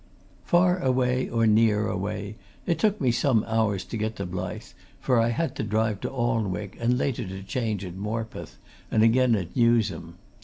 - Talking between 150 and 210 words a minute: Yes, average, 180 wpm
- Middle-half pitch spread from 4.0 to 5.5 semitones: No, average, 3.3 semitones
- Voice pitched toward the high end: No, low, 110 Hz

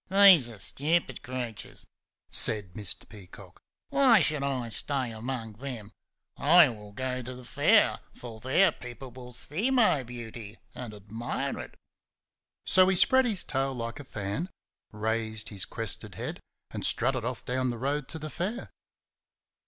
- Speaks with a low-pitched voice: Yes, low, 125 Hz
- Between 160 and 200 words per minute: No, average, 150 wpm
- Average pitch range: Yes, average, 4.8 semitones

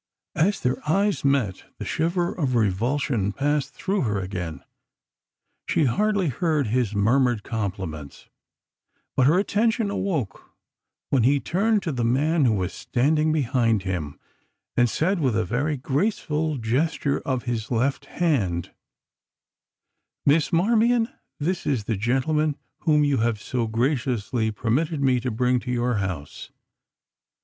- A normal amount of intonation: No, wide, 5.8 semitones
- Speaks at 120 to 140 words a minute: Yes, slow, 135 wpm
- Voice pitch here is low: Yes, low, 130 Hz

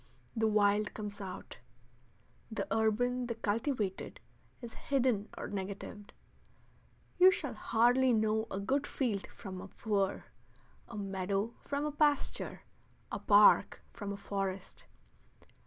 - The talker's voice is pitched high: Yes, high, 215 Hz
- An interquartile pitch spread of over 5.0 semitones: No, average, 3.5 semitones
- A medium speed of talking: No, slow, 125 wpm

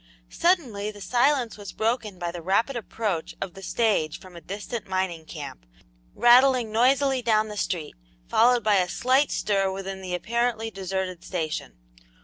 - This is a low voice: No, high, 210 Hz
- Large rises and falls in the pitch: No, average, 4.2 semitones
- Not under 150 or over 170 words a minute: Yes, average, 155 wpm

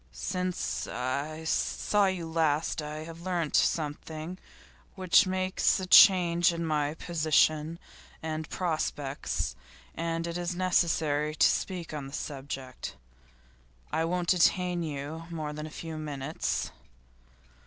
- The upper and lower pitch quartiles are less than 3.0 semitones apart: Yes, narrow, 2.6 semitones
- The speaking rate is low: Yes, slow, 120 wpm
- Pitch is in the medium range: Yes, medium, 160 Hz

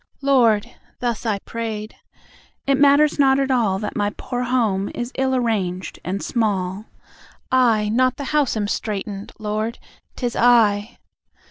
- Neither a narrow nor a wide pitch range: Yes, average, 3.6 semitones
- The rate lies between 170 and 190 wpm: No, average, 140 wpm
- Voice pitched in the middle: No, high, 230 Hz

